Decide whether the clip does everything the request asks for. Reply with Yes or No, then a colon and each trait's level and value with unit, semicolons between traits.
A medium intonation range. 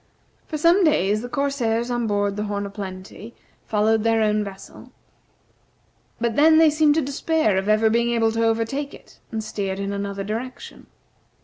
Yes: average, 4.8 semitones